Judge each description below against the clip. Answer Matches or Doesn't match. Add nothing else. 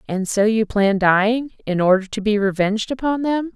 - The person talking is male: Doesn't match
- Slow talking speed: Doesn't match